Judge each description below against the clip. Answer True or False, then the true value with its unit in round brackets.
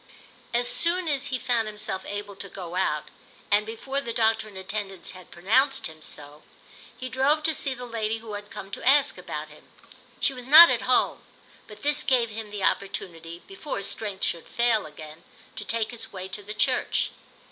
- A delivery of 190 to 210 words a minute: True (195 wpm)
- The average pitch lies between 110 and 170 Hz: False (220 Hz)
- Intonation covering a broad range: False (5.0 semitones)